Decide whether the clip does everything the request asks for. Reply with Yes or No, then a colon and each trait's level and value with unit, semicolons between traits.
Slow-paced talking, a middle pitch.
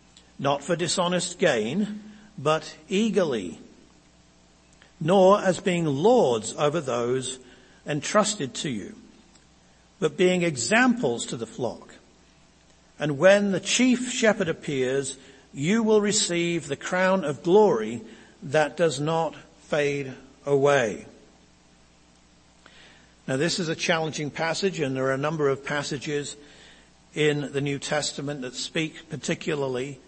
Yes: slow, 120 wpm; medium, 150 Hz